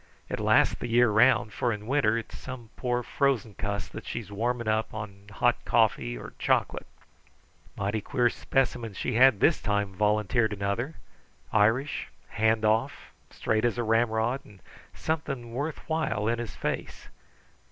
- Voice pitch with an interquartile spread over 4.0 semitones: No, average, 2.7 semitones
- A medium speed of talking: Yes, average, 150 wpm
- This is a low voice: Yes, low, 115 Hz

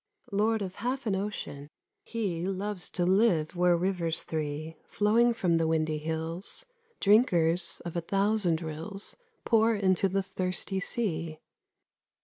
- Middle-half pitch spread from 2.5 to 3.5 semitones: No, average, 4.1 semitones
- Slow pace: Yes, slow, 130 wpm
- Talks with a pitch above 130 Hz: Yes, medium, 185 Hz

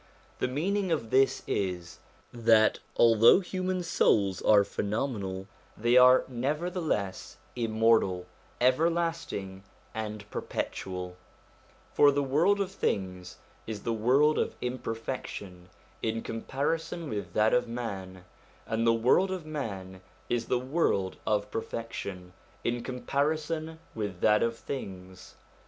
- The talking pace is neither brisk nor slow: No, slow, 120 wpm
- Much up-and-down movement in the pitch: Yes, wide, 6.2 semitones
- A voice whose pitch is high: No, low, 115 Hz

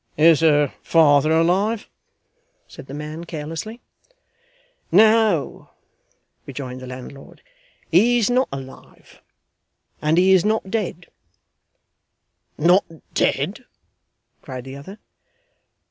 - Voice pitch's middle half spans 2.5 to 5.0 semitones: No, wide, 5.5 semitones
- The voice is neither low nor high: Yes, medium, 165 Hz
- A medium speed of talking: No, slow, 100 wpm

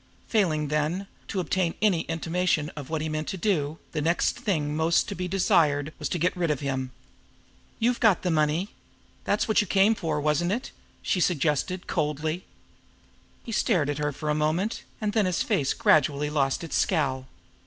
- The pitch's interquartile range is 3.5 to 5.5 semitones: Yes, average, 3.8 semitones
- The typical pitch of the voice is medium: Yes, medium, 160 Hz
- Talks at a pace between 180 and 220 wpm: Yes, average, 185 wpm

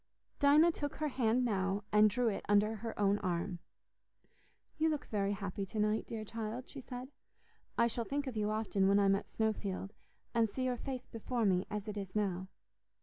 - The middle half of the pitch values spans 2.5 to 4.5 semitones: Yes, average, 3.7 semitones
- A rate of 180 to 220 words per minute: Yes, average, 195 wpm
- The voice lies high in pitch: Yes, high, 215 Hz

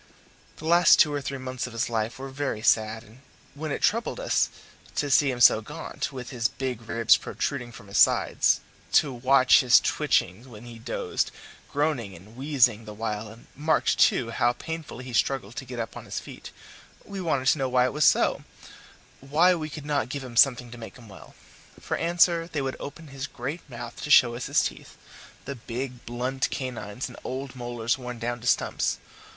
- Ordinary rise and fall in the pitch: Yes, average, 3.4 semitones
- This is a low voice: Yes, low, 125 Hz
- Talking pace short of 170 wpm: No, average, 200 wpm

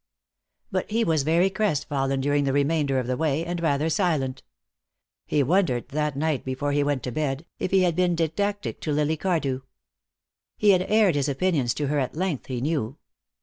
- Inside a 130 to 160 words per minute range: No, average, 190 wpm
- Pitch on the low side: No, medium, 150 Hz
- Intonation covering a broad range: No, average, 4.1 semitones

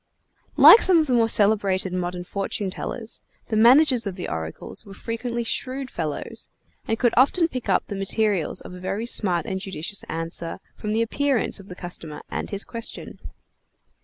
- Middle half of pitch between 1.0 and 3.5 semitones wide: No, average, 4.5 semitones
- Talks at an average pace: Yes, average, 180 wpm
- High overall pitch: Yes, high, 210 Hz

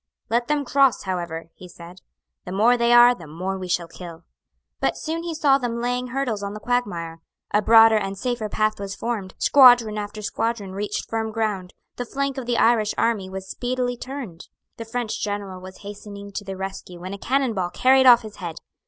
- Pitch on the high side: Yes, high, 215 Hz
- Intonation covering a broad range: No, average, 4.3 semitones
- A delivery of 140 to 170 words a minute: No, average, 200 wpm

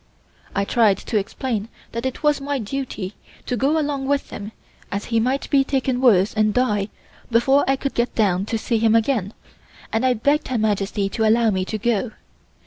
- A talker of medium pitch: No, high, 230 Hz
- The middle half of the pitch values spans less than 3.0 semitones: No, average, 4.1 semitones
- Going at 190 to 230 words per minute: Yes, average, 195 wpm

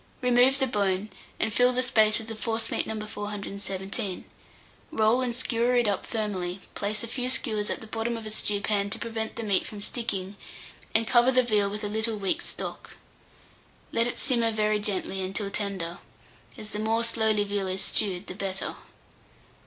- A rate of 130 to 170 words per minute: No, average, 180 wpm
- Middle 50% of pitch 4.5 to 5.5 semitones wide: No, narrow, 2.4 semitones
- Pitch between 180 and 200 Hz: No, high, 215 Hz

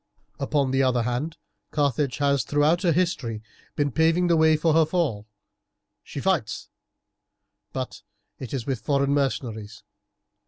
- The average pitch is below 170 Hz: Yes, medium, 140 Hz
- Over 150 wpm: No, average, 140 wpm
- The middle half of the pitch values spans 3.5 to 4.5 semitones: Yes, average, 4.1 semitones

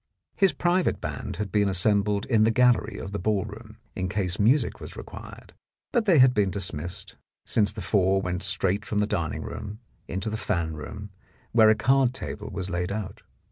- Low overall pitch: Yes, low, 105 Hz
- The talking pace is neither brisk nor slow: Yes, average, 185 wpm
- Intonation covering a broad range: No, average, 2.7 semitones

